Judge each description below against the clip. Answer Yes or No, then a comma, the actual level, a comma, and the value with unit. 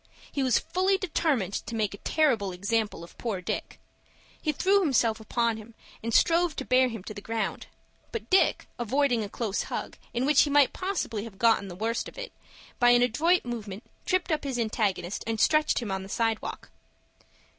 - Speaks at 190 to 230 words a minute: Yes, average, 195 wpm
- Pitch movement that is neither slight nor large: No, wide, 5.7 semitones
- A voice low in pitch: No, high, 235 Hz